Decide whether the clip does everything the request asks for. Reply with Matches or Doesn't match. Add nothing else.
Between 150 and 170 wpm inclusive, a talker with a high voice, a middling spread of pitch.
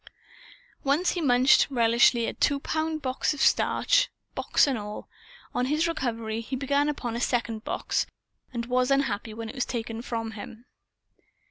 Matches